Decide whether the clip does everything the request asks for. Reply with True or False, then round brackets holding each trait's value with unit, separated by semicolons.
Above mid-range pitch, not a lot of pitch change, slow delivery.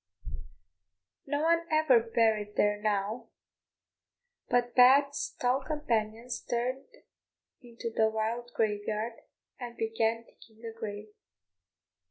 True (230 Hz; 2.3 semitones; 100 wpm)